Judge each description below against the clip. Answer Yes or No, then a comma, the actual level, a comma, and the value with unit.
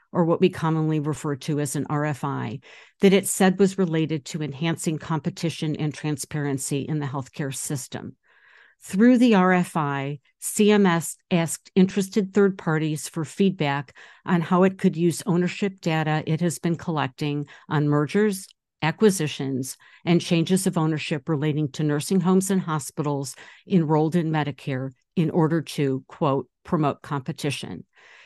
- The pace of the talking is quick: No, average, 140 wpm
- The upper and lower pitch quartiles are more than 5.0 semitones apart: No, average, 3.8 semitones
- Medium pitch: Yes, medium, 160 Hz